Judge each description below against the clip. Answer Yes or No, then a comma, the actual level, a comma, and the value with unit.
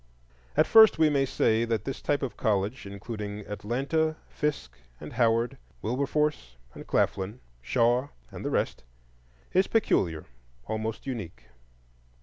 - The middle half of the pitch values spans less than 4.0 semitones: No, average, 5.3 semitones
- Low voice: Yes, low, 115 Hz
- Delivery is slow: Yes, slow, 130 wpm